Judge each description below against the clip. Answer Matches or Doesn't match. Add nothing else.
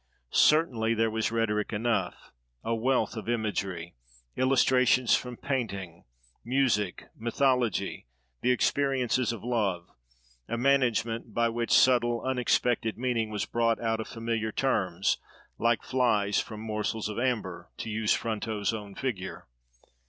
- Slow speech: Matches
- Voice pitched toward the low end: Matches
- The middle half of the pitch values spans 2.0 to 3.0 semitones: Matches